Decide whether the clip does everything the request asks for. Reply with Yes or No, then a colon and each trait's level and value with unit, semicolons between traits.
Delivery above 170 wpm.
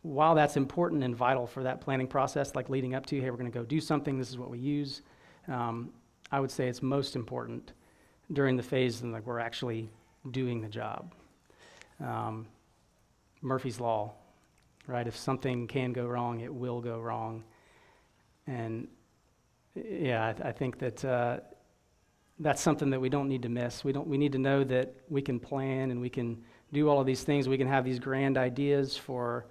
Yes: average, 195 wpm